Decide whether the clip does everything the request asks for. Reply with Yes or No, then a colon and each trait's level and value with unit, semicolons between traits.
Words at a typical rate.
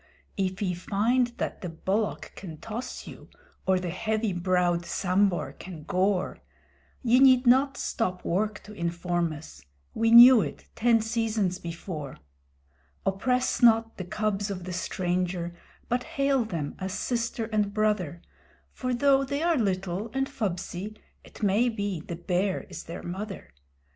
Yes: average, 150 wpm